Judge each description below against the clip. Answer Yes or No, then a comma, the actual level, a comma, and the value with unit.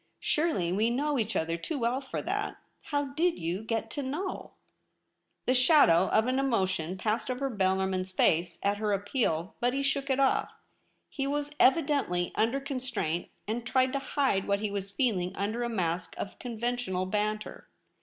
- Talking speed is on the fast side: No, average, 175 wpm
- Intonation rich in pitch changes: Yes, wide, 6.1 semitones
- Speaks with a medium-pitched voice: No, high, 230 Hz